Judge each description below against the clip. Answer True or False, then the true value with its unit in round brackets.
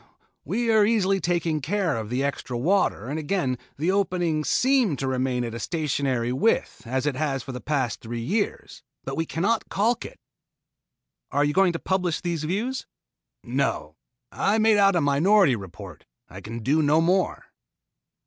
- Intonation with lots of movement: True (6.9 semitones)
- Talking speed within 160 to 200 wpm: True (170 wpm)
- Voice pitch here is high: False (155 Hz)